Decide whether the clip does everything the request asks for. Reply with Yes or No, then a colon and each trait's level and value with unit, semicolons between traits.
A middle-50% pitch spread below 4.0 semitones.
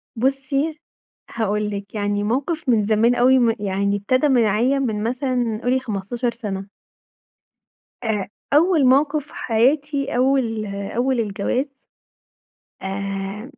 No: average, 4.3 semitones